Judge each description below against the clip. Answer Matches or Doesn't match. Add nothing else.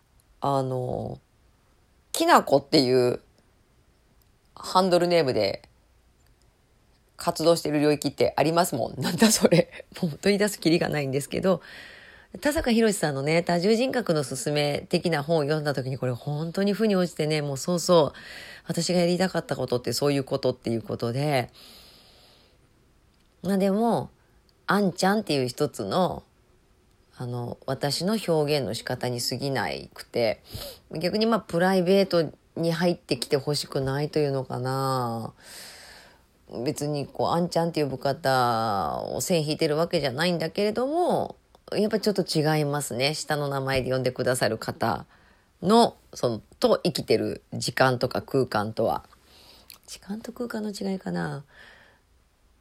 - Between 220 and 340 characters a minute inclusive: Matches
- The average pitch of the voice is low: Doesn't match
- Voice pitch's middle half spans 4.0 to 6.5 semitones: Matches